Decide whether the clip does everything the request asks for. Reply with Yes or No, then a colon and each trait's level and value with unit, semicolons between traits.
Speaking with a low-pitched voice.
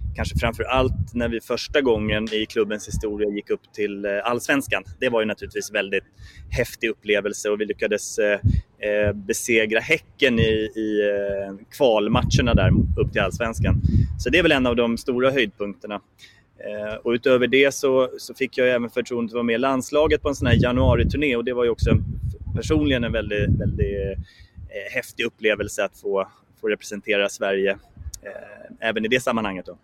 Yes: low, 110 Hz